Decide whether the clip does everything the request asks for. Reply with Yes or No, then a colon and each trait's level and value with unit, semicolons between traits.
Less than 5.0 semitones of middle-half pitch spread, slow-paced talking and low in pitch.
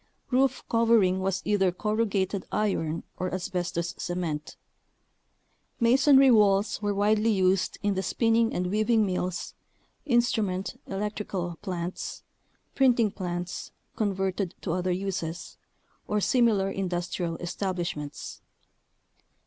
No: average, 3.1 semitones; slow, 100 wpm; high, 195 Hz